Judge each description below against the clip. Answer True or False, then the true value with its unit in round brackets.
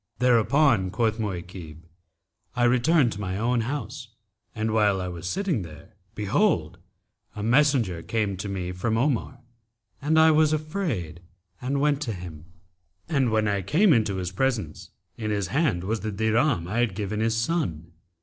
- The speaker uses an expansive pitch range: True (6.2 semitones)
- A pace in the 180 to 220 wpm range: False (160 wpm)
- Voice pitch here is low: True (110 Hz)